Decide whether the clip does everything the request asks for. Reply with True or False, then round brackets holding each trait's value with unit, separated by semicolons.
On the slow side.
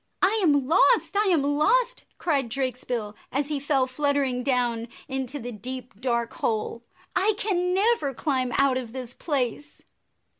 False (155 wpm)